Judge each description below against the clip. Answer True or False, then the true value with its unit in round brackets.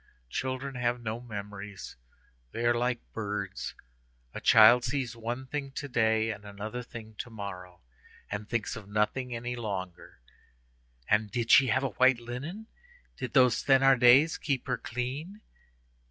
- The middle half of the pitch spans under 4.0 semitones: True (3.2 semitones)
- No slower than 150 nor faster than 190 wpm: False (140 wpm)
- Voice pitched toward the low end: True (120 Hz)